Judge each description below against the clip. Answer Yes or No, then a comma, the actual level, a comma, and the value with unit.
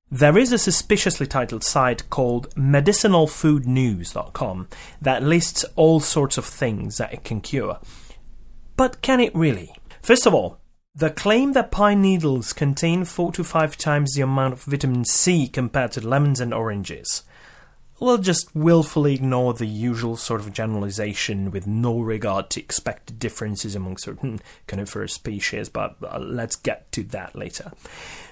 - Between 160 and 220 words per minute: No, average, 150 wpm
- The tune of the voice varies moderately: No, wide, 6.5 semitones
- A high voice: No, low, 135 Hz